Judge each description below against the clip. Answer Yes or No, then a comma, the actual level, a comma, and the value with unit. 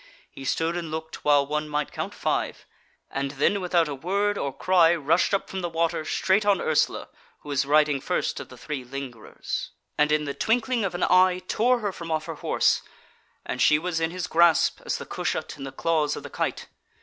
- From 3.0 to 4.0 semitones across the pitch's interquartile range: Yes, average, 3.7 semitones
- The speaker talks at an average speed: No, fast, 210 wpm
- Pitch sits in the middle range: Yes, medium, 160 Hz